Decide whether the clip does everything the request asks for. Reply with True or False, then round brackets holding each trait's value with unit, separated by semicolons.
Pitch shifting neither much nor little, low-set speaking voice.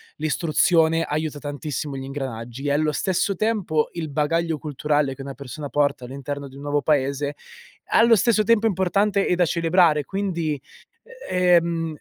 False (3.7 semitones; 155 Hz)